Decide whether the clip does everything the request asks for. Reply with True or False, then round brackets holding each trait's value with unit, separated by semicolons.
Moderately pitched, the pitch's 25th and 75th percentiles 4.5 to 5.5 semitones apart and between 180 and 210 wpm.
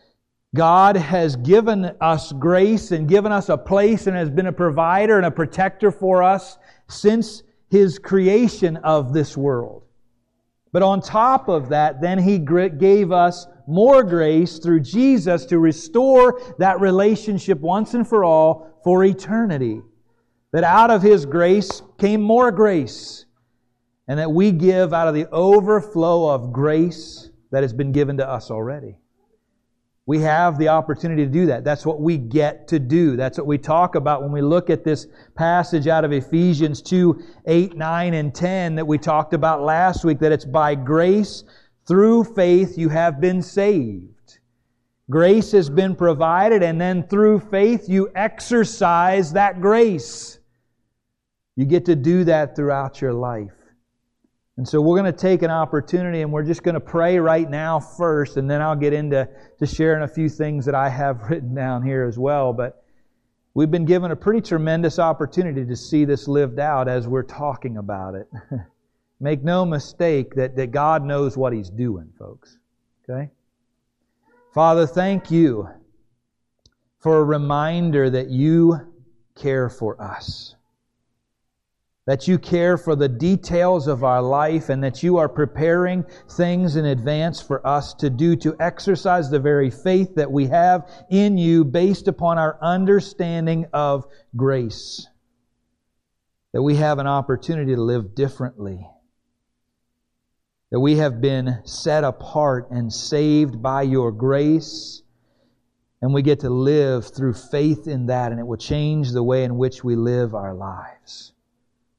False (155 Hz; 5.2 semitones; 160 wpm)